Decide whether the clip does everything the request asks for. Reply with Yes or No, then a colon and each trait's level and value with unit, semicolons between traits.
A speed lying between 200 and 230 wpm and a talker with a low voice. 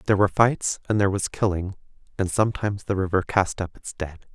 Yes: fast, 205 wpm; very low, 95 Hz